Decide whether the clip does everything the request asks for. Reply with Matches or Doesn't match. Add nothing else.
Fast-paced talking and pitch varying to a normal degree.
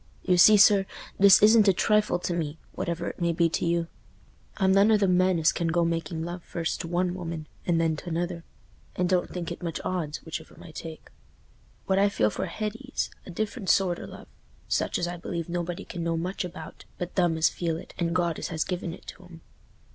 Doesn't match